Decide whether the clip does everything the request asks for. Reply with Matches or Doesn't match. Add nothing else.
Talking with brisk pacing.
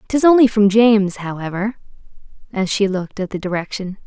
Doesn't match